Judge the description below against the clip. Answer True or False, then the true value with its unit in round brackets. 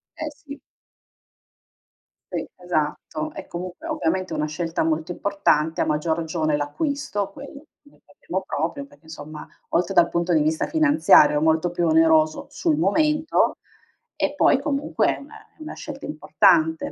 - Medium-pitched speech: True (175 Hz)